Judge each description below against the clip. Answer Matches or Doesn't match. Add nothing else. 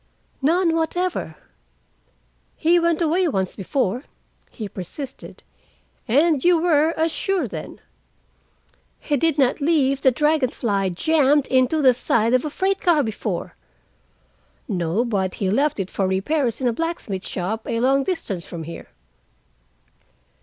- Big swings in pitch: Matches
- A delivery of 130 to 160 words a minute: Matches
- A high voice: Matches